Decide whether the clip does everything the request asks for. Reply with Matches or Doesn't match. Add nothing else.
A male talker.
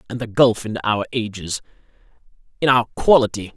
Matches